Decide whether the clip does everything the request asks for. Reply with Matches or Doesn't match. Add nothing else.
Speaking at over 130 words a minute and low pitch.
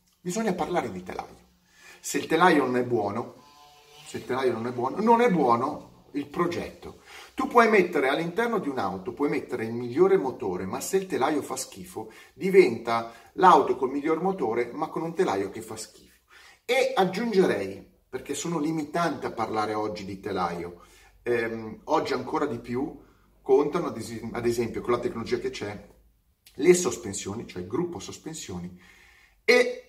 Doesn't match